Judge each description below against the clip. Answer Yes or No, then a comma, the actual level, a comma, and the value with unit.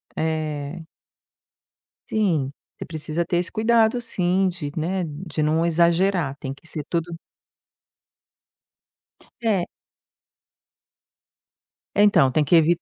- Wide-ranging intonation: No, average, 3.3 semitones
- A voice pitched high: No, medium, 170 Hz